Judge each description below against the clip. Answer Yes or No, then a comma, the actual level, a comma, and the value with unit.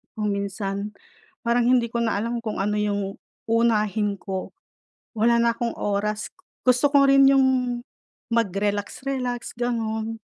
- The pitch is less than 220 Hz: No, high, 225 Hz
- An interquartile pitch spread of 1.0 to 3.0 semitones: Yes, average, 2.7 semitones